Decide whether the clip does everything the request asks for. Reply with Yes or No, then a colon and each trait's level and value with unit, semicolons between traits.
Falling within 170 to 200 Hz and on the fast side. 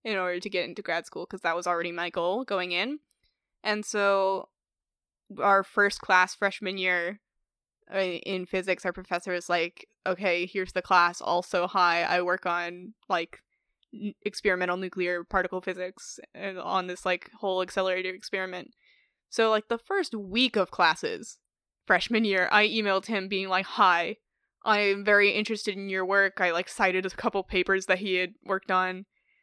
No: high, 190 Hz; average, 165 wpm